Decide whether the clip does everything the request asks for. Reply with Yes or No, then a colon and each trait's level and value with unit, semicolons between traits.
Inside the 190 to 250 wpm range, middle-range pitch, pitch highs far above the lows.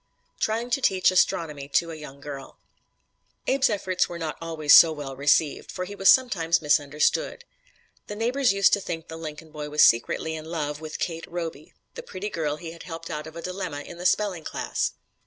No: average, 195 wpm; medium, 165 Hz; average, 3.8 semitones